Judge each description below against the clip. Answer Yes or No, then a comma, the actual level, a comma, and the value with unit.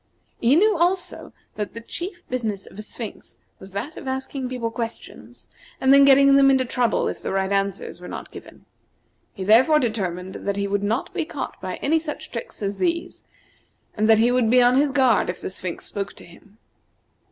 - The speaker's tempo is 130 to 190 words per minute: No, average, 200 wpm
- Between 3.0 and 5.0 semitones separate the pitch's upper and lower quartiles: No, wide, 5.5 semitones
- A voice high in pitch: Yes, high, 240 Hz